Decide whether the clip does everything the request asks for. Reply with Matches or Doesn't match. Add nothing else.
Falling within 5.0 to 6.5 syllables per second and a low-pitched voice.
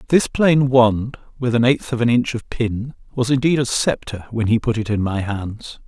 Doesn't match